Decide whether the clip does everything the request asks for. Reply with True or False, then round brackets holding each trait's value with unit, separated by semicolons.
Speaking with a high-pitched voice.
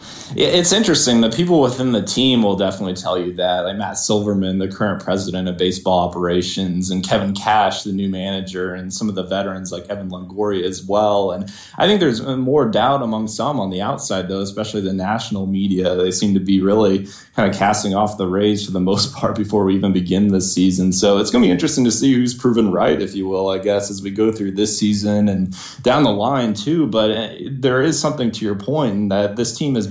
False (100 Hz)